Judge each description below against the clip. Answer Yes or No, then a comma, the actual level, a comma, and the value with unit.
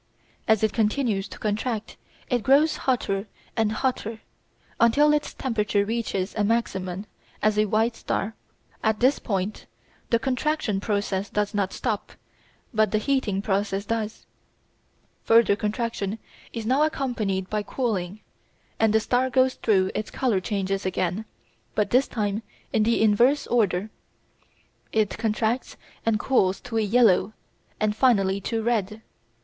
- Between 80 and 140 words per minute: Yes, slow, 135 wpm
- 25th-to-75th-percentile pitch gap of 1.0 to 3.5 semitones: Yes, average, 2.7 semitones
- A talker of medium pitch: No, high, 215 Hz